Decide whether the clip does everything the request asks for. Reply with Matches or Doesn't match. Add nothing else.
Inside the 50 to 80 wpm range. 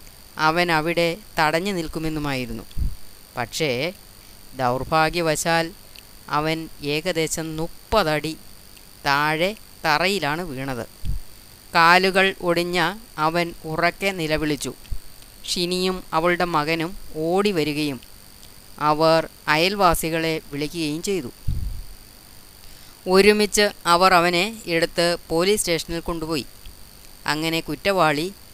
Matches